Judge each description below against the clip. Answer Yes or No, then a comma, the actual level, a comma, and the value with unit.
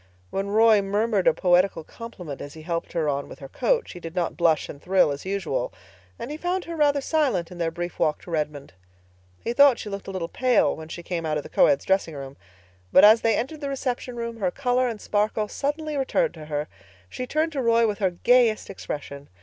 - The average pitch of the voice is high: Yes, high, 200 Hz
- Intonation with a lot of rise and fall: Yes, wide, 7.0 semitones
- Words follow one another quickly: Yes, fast, 225 wpm